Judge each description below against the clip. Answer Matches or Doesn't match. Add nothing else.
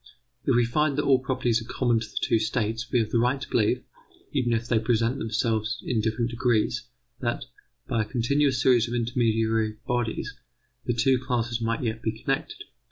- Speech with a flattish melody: Matches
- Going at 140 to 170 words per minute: Doesn't match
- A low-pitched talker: Matches